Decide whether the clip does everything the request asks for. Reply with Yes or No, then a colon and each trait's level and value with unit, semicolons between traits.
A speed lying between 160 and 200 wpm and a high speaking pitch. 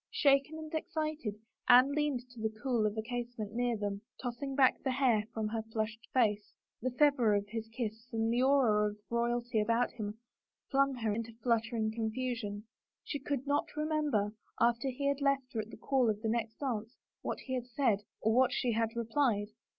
Yes: average, 195 wpm; high, 235 Hz